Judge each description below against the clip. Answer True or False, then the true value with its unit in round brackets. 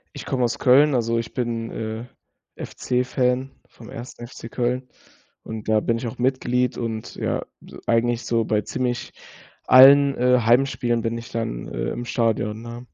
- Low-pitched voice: True (120 Hz)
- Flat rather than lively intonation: True (1.6 semitones)